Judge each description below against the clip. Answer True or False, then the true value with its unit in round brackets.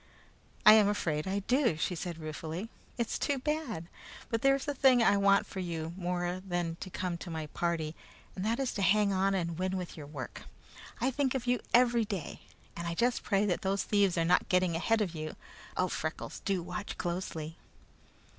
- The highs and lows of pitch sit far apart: False (4.5 semitones)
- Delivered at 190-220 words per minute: True (200 wpm)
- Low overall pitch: False (185 Hz)